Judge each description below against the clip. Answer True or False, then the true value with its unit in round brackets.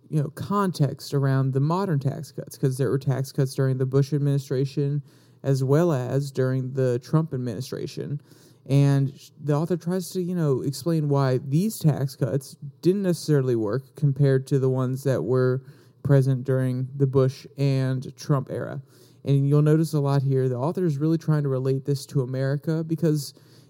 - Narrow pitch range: True (2.2 semitones)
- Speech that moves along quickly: False (175 wpm)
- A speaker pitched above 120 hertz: True (140 Hz)